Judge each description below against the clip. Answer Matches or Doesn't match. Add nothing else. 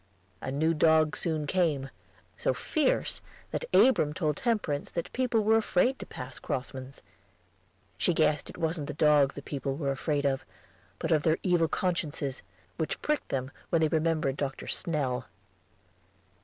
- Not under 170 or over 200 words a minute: Doesn't match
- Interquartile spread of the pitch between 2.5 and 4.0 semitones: Matches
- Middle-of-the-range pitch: Matches